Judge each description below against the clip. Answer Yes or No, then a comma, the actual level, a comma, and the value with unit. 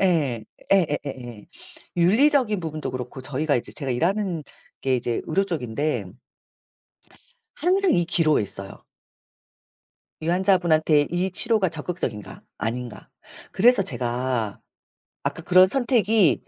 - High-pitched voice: No, medium, 160 Hz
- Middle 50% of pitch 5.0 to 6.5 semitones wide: No, wide, 7.0 semitones